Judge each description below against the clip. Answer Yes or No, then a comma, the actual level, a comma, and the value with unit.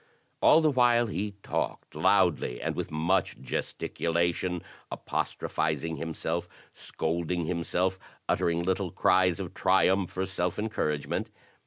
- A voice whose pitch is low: Yes, very low, 90 Hz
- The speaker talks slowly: Yes, slow, 120 wpm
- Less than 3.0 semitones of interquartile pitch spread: Yes, narrow, 2.5 semitones